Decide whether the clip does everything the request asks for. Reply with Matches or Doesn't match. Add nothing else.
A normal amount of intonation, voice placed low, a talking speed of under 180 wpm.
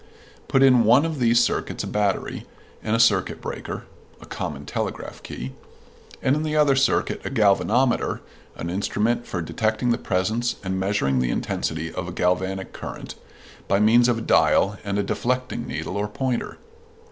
Matches